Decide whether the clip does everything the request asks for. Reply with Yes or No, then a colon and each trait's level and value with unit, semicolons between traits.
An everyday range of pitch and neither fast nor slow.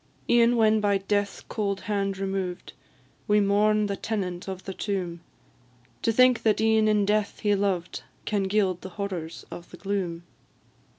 No: narrow, 1.9 semitones; average, 160 wpm